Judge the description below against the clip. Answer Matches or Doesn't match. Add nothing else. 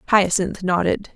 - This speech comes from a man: Doesn't match